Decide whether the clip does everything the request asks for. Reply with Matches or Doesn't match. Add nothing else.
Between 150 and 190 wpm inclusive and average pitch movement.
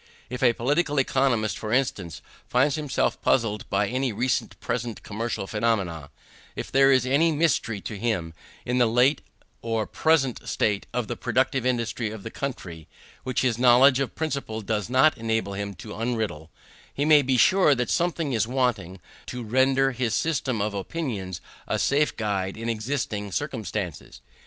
Matches